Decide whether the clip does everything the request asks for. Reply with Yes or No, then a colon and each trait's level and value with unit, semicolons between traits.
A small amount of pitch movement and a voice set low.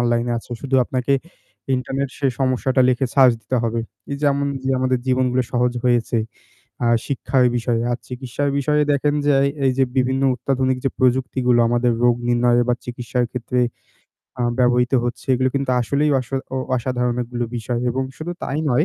Yes: narrow, 1.7 semitones; low, 125 Hz